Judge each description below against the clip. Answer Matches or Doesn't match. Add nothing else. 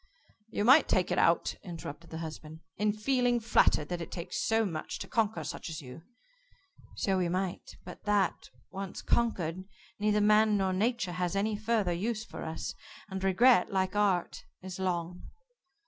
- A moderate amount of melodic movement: Matches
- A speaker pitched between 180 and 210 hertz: Matches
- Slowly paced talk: Doesn't match